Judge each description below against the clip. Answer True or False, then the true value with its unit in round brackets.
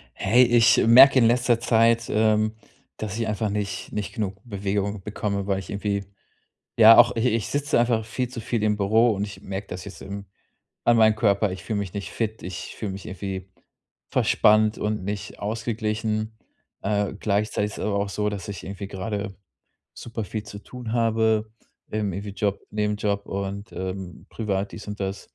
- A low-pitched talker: True (105 Hz)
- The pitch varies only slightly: True (2.0 semitones)